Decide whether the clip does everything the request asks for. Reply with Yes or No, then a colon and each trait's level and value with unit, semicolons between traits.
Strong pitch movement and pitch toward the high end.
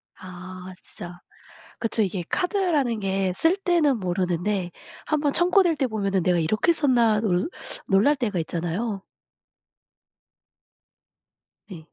Yes: wide, 7.7 semitones; high, 210 Hz